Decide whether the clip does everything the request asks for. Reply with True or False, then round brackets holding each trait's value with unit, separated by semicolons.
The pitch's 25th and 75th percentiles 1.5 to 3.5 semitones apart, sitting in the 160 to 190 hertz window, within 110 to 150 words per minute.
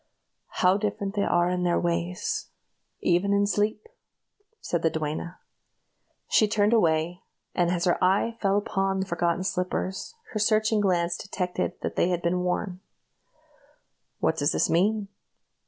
True (2.8 semitones; 185 Hz; 145 wpm)